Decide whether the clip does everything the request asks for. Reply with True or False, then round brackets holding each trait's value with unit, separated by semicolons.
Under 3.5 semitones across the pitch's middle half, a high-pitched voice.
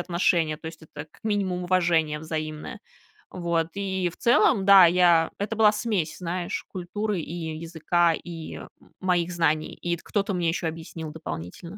False (2.4 semitones; 170 Hz)